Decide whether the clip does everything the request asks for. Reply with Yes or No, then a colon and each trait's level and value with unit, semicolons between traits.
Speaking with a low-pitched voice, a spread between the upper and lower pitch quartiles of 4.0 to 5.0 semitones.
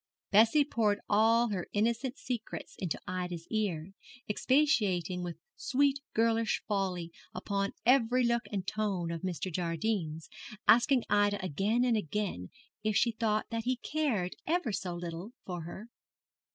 No: high, 210 Hz; average, 4.6 semitones